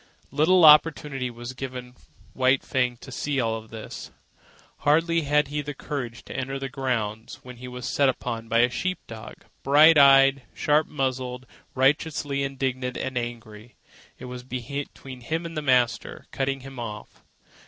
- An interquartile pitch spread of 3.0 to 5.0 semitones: No, narrow, 2.6 semitones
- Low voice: Yes, low, 130 Hz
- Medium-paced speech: Yes, average, 150 wpm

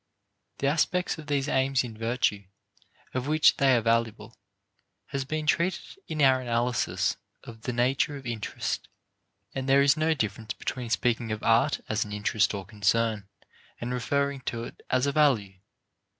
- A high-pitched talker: No, low, 125 Hz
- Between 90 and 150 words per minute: No, average, 165 wpm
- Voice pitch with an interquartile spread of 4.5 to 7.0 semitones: No, average, 3.7 semitones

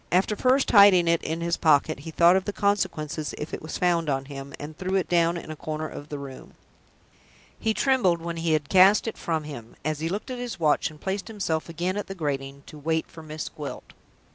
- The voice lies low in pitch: No, medium, 165 Hz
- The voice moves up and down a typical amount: Yes, average, 3.9 semitones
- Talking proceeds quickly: Yes, fast, 230 wpm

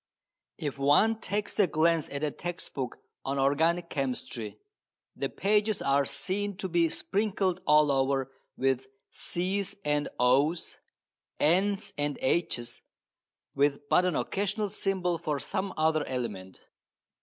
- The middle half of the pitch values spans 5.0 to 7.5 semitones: Yes, wide, 5.4 semitones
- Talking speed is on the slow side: Yes, slow, 130 wpm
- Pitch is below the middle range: No, medium, 160 Hz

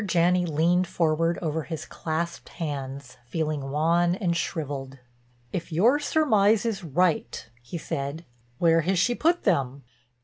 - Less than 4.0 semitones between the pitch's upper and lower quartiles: Yes, average, 3.5 semitones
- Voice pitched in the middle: Yes, medium, 165 Hz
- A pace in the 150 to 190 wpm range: No, slow, 135 wpm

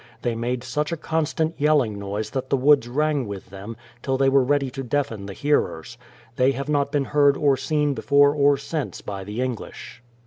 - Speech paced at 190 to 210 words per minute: Yes, average, 200 wpm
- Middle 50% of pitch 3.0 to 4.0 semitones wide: Yes, average, 3.6 semitones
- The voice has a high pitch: No, low, 135 Hz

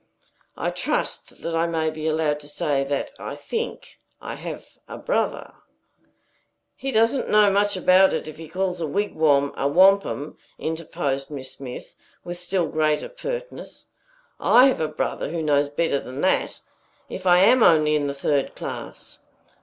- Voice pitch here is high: No, medium, 160 Hz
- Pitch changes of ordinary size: Yes, average, 4.7 semitones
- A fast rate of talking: No, average, 160 wpm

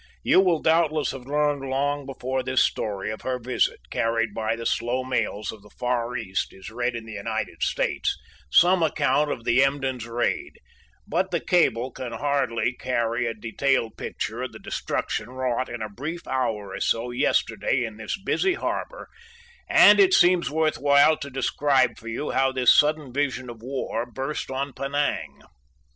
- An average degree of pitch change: Yes, average, 3.5 semitones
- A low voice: Yes, low, 130 Hz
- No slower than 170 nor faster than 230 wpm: Yes, average, 175 wpm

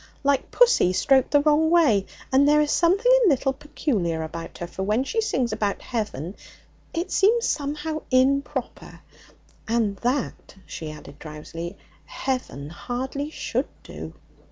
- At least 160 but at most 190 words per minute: No, average, 140 wpm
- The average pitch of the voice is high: Yes, very high, 260 Hz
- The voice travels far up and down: Yes, wide, 7.3 semitones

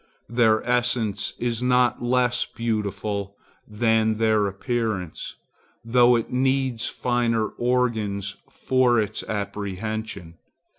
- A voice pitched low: Yes, low, 115 Hz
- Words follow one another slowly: Yes, slow, 95 wpm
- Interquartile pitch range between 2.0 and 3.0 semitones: Yes, average, 2.7 semitones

